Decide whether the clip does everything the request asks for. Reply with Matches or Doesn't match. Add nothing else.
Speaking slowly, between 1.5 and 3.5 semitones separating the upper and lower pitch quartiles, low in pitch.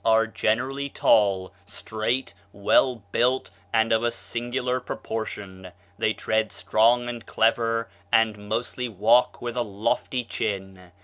Matches